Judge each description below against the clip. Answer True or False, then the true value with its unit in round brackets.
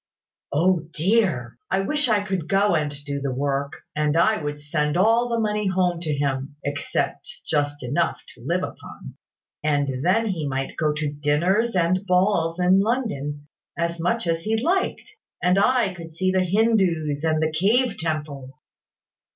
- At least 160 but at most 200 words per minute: True (165 wpm)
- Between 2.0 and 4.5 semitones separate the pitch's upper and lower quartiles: False (5.2 semitones)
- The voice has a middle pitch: True (170 Hz)